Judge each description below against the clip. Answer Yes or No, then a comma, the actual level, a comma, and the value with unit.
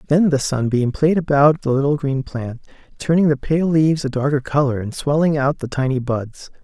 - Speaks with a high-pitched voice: No, medium, 140 Hz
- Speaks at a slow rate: No, average, 200 wpm